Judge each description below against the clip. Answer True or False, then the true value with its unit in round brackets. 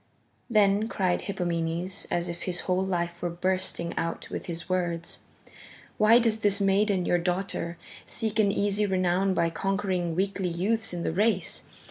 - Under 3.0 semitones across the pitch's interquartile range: True (2.6 semitones)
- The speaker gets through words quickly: False (155 wpm)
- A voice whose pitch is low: False (185 Hz)